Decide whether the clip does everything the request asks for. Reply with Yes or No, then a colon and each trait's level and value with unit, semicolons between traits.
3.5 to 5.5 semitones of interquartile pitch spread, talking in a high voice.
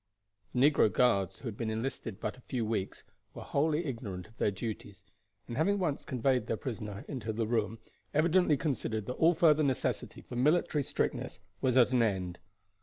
No: average, 4.7 semitones; low, 125 Hz